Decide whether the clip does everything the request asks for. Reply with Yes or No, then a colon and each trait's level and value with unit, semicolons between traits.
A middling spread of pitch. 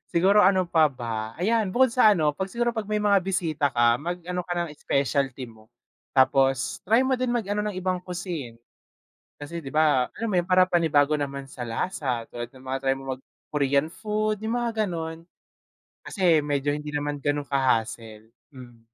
No: wide, 5.9 semitones